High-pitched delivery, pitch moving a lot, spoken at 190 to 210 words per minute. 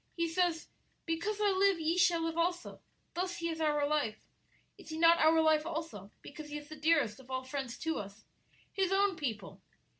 No: very high, 320 Hz; average, 2.8 semitones; average, 200 wpm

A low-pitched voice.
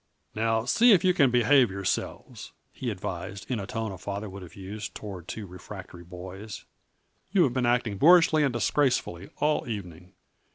Yes: low, 110 Hz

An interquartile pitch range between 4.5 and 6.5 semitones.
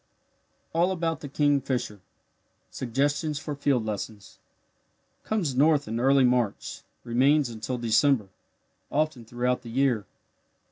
No: average, 3.7 semitones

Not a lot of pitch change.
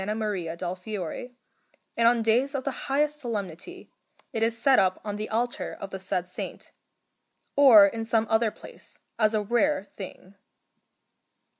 No: average, 3.7 semitones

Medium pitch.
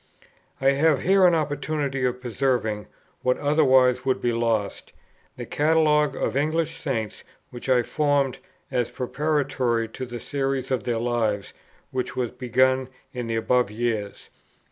No: low, 130 Hz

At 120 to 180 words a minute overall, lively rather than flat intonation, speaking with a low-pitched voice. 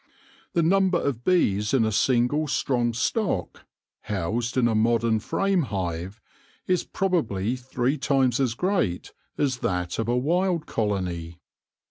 Yes: slow, 135 wpm; wide, 6.5 semitones; low, 120 Hz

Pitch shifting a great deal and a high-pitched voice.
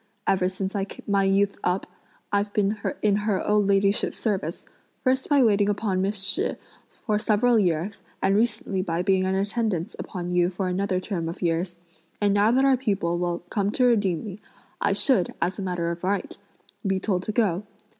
No: narrow, 2.5 semitones; high, 195 Hz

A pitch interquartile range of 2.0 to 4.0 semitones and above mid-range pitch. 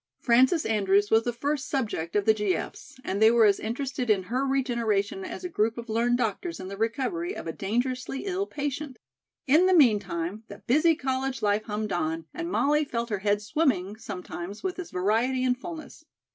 No: average, 4.8 semitones; high, 235 Hz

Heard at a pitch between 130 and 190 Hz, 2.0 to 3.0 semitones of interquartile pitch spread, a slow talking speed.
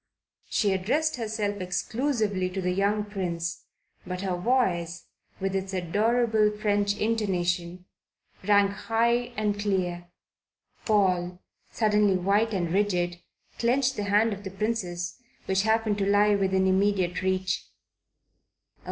No: high, 200 Hz; average, 2.7 semitones; slow, 120 wpm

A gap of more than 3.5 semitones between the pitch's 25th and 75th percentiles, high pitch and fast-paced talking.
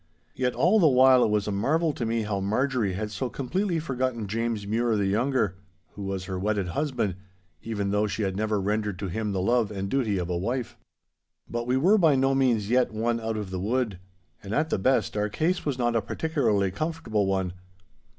No: average, 4.5 semitones; low, 110 Hz; fast, 210 wpm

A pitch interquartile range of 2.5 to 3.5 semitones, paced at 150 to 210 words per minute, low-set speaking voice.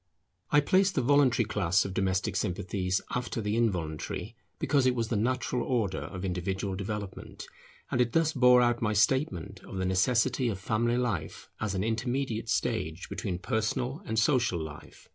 No: average, 4.8 semitones; average, 165 wpm; low, 110 Hz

